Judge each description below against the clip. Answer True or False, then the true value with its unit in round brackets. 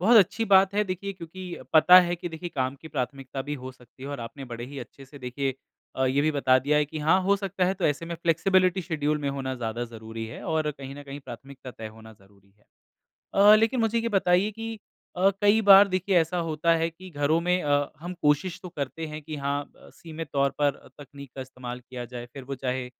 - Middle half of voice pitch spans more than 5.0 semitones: True (5.6 semitones)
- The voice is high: False (150 Hz)